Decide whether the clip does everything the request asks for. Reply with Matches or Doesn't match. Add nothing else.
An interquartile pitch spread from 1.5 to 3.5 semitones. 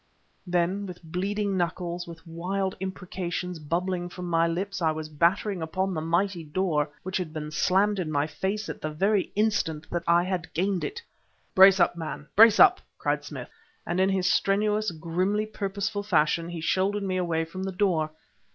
Matches